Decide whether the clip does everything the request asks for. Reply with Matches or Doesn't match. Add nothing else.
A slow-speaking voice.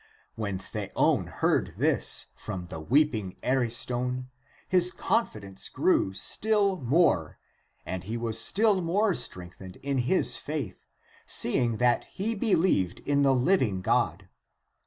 Matches